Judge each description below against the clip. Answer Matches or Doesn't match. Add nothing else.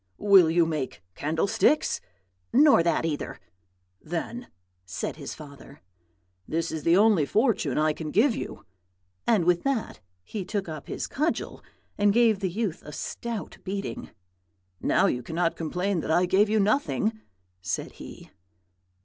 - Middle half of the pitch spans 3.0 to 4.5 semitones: Doesn't match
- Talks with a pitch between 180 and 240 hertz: Matches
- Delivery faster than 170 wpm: Doesn't match